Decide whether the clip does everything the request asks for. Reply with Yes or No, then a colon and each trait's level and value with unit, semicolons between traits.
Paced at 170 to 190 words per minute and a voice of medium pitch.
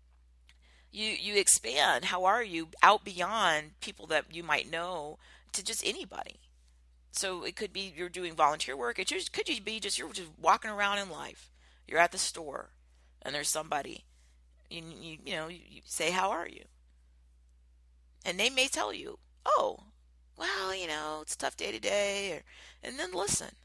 Yes: average, 180 wpm; medium, 155 Hz